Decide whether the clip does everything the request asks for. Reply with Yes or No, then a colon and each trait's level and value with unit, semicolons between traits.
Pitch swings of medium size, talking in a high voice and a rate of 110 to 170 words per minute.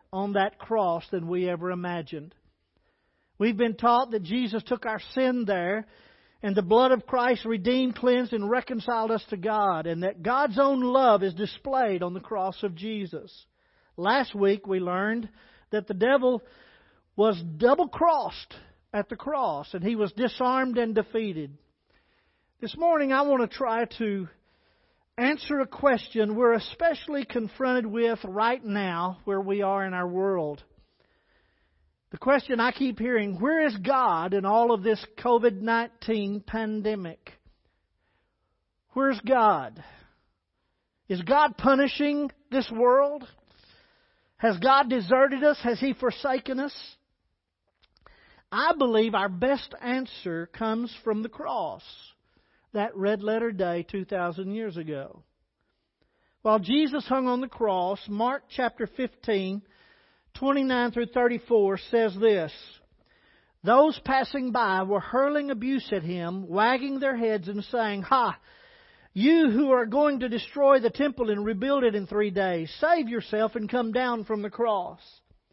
Yes: average, 4.4 semitones; high, 230 Hz; average, 140 wpm